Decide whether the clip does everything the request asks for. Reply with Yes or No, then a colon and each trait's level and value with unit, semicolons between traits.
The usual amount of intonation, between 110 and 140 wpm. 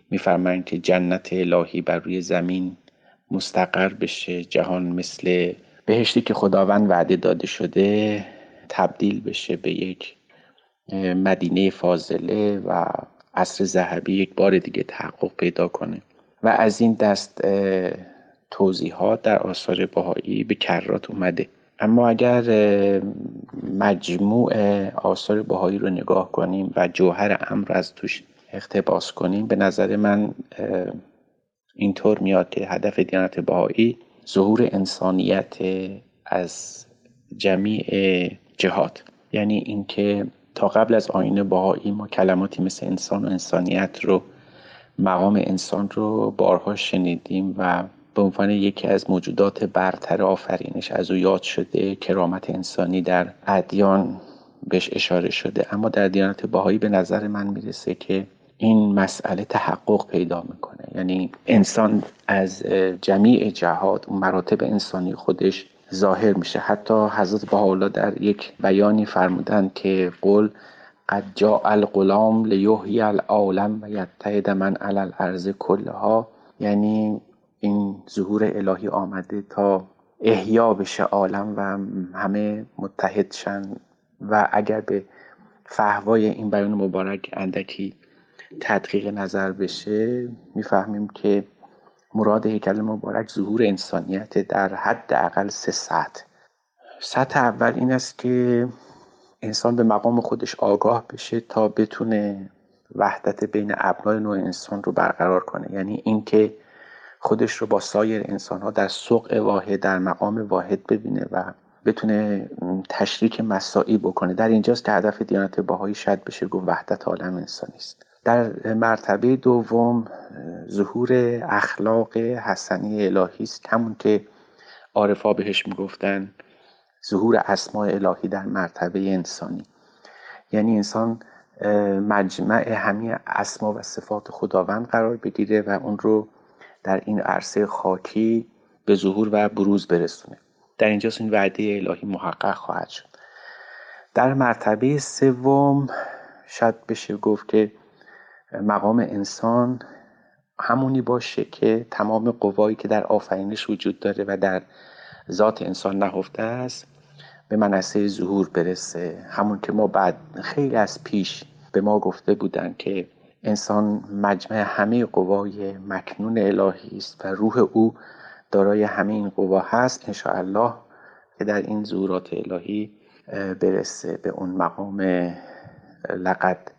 No: narrow, 2.1 semitones; average, 125 wpm